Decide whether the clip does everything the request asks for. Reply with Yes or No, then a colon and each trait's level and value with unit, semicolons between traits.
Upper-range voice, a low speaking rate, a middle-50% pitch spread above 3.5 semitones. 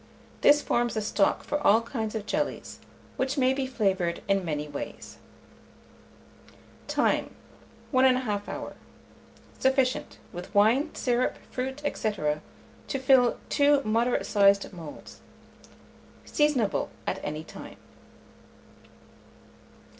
Yes: high, 230 Hz; slow, 110 wpm; average, 4.9 semitones